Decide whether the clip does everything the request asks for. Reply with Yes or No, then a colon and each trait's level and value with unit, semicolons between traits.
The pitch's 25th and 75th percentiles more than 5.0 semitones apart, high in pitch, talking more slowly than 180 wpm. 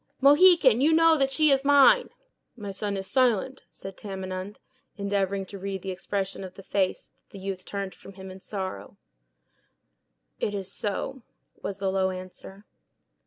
Yes: wide, 5.4 semitones; high, 200 Hz; average, 165 wpm